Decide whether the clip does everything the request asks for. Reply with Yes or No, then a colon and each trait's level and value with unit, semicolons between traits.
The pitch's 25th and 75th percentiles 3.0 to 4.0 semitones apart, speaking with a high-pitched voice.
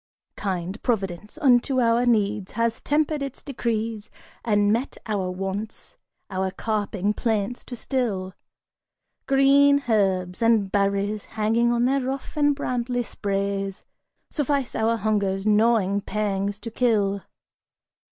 Yes: average, 3.6 semitones; high, 215 Hz